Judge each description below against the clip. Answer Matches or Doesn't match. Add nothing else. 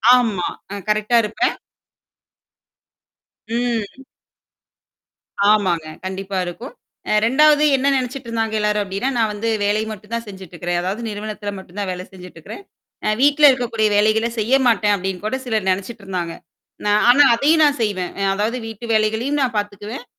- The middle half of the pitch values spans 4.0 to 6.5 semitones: Doesn't match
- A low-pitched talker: Doesn't match